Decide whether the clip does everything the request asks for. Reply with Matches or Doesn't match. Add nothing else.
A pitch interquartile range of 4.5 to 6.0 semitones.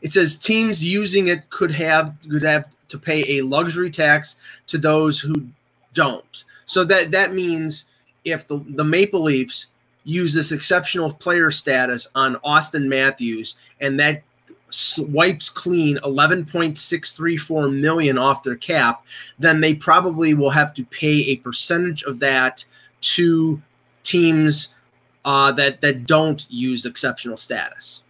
Doesn't match